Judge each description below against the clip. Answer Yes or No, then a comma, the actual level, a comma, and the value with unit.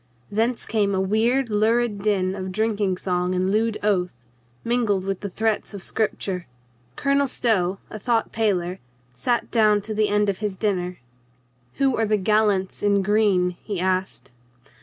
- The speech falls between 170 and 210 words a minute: No, average, 160 wpm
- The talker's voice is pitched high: Yes, high, 205 Hz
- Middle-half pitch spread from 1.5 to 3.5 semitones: Yes, average, 2.7 semitones